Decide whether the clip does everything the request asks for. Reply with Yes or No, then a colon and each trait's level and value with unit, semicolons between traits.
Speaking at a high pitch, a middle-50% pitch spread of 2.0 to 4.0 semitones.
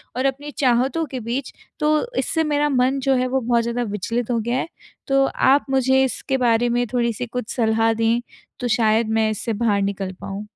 Yes: high, 245 Hz; average, 2.8 semitones